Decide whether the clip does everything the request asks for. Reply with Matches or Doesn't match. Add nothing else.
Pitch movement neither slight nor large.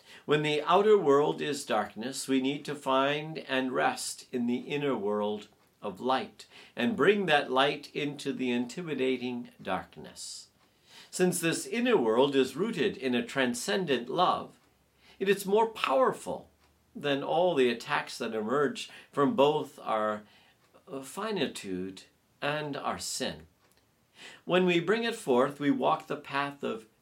Matches